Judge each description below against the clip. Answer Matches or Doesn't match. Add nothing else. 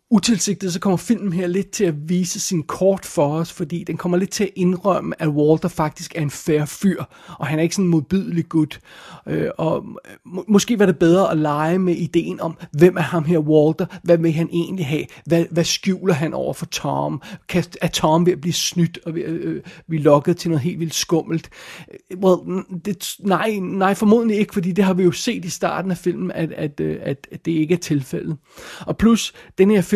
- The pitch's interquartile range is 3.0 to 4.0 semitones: Doesn't match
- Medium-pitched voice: Matches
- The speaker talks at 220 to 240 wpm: Matches